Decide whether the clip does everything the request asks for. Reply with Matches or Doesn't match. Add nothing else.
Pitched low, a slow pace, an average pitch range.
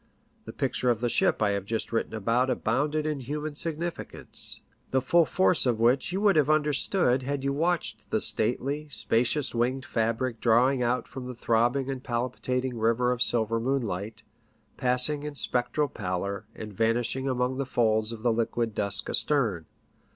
Doesn't match